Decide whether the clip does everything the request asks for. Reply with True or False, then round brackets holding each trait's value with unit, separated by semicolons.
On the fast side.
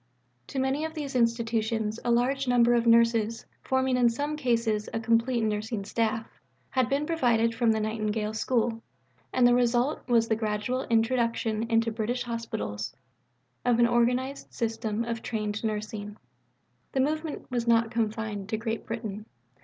False (155 wpm)